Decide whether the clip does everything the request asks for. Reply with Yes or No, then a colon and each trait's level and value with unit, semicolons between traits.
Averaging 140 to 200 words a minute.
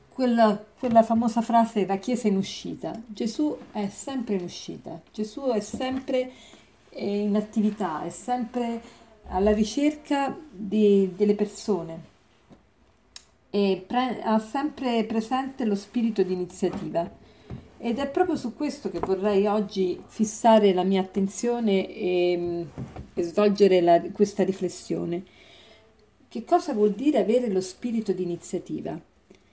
No: average, 120 wpm